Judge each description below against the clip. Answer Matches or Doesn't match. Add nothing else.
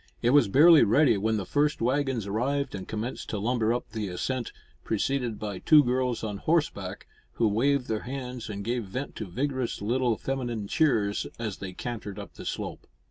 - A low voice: Matches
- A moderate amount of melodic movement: Matches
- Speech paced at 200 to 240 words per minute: Doesn't match